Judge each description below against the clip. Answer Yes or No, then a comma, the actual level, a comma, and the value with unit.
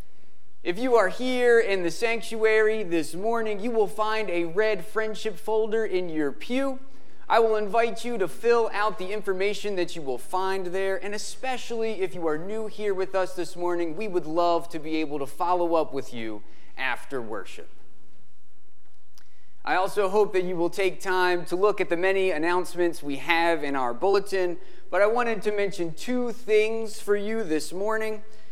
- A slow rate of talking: No, average, 185 wpm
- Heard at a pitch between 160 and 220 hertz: Yes, high, 190 Hz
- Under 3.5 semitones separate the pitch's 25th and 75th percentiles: No, average, 4.3 semitones